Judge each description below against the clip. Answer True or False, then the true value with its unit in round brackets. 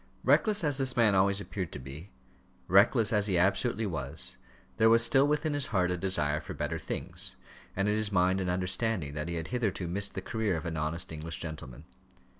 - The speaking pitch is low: True (95 Hz)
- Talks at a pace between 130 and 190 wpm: False (205 wpm)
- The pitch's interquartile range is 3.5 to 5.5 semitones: True (5.1 semitones)